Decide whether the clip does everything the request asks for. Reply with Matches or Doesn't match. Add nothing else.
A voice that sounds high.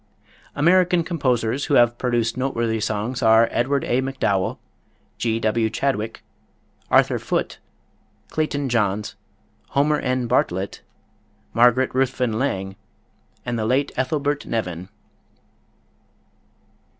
Doesn't match